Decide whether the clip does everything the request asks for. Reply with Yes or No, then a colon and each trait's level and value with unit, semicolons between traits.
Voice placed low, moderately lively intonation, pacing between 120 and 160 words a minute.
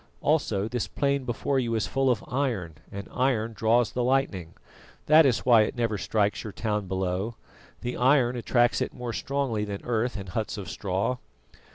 No: low, 115 Hz; average, 3.5 semitones; average, 180 wpm